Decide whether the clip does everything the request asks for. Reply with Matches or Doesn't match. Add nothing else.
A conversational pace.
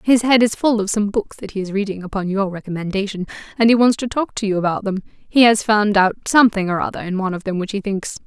Doesn't match